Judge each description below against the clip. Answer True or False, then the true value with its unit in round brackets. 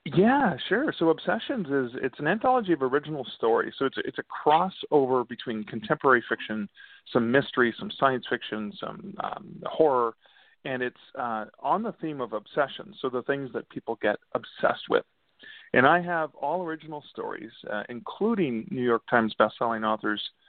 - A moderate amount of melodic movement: False (5.9 semitones)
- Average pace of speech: True (165 wpm)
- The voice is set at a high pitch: False (135 Hz)